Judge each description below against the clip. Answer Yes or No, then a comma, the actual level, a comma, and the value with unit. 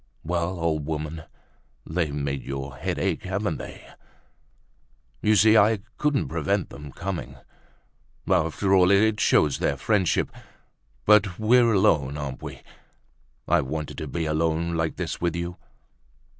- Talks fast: No, average, 140 wpm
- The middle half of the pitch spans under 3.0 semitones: No, average, 4.6 semitones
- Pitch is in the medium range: No, very low, 85 Hz